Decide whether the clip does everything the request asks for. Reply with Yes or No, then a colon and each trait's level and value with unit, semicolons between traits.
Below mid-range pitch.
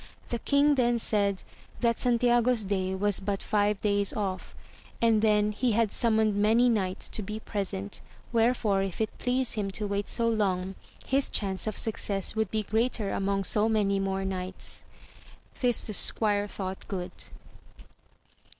No: high, 210 Hz